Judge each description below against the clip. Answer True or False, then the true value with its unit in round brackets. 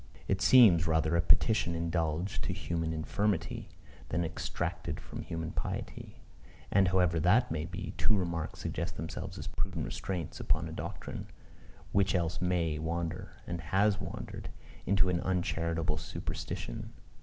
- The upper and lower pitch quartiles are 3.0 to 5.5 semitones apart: False (2.5 semitones)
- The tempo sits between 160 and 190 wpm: False (140 wpm)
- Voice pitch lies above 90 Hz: False (85 Hz)